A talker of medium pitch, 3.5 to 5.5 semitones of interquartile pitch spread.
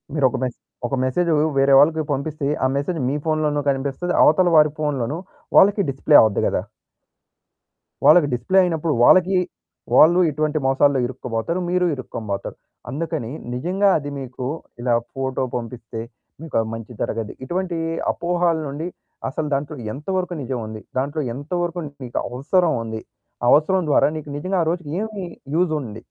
Yes: medium, 145 Hz; average, 4.9 semitones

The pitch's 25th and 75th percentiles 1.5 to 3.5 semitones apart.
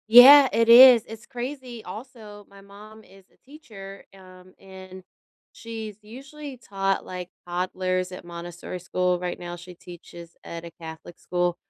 No: average, 4.2 semitones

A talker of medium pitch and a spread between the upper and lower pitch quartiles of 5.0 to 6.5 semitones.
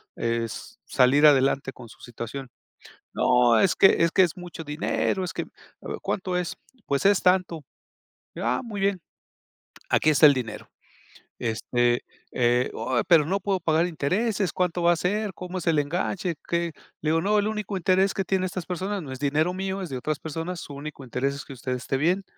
Yes: medium, 165 Hz; wide, 5.5 semitones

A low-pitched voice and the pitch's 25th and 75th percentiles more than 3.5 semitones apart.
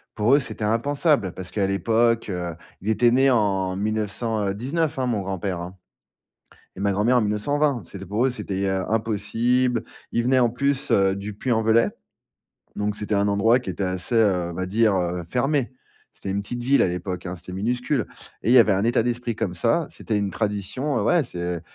Yes: low, 110 Hz; average, 4.1 semitones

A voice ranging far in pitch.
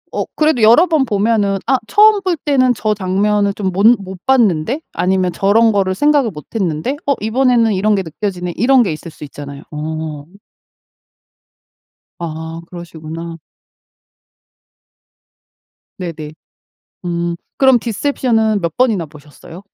Yes: wide, 6.2 semitones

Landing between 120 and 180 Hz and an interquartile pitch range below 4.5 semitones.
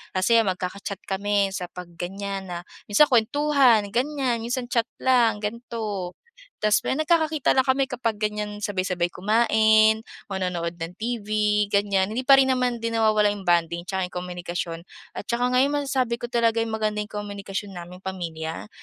No: high, 210 Hz; average, 3.9 semitones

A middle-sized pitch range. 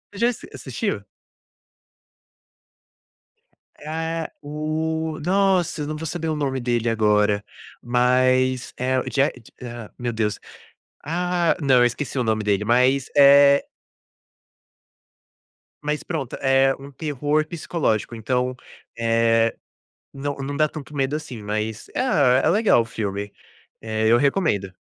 Yes: average, 4.7 semitones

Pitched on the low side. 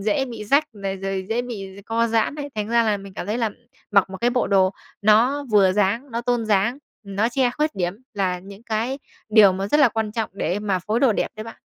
No: high, 215 Hz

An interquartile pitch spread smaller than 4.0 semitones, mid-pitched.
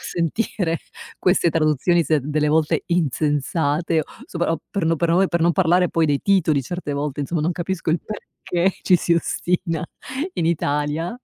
Yes: average, 2.7 semitones; medium, 165 Hz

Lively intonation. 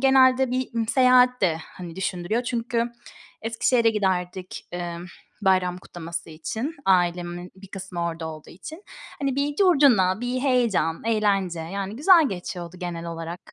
Yes: wide, 6.1 semitones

